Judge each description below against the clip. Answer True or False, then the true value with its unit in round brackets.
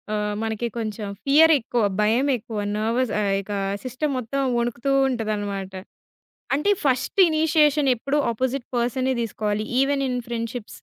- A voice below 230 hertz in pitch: False (240 Hz)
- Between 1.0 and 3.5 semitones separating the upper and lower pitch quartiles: False (4.1 semitones)